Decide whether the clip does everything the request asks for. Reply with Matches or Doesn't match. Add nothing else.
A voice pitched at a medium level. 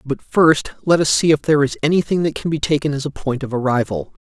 Matches